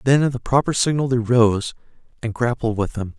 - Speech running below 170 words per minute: No, fast, 205 wpm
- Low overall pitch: Yes, low, 120 Hz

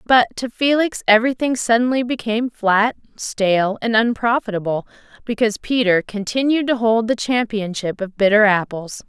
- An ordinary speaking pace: No, slow, 130 wpm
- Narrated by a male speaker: No, female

